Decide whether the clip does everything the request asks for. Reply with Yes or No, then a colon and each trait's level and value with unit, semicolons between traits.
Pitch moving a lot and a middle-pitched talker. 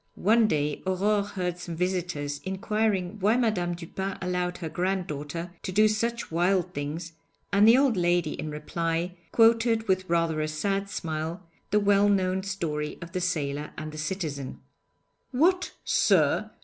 No: average, 3.7 semitones; medium, 180 Hz